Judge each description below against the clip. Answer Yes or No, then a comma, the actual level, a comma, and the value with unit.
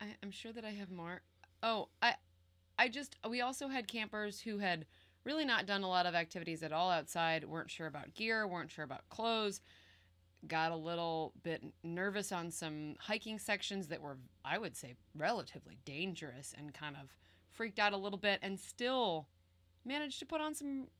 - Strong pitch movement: Yes, wide, 6.2 semitones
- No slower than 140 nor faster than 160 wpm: No, average, 185 wpm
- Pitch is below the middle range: No, medium, 180 Hz